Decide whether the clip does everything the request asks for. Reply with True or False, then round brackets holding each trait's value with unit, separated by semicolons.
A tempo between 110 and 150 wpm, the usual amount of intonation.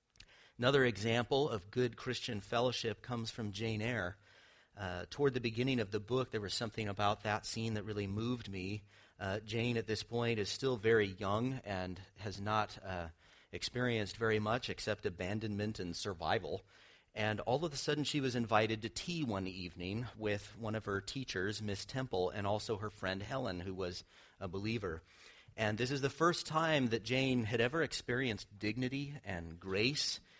False (175 wpm; 3.6 semitones)